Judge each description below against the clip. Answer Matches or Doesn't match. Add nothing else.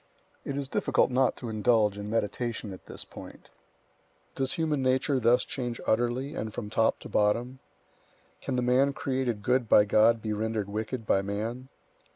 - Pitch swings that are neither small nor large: Matches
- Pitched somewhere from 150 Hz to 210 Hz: Doesn't match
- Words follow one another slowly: Doesn't match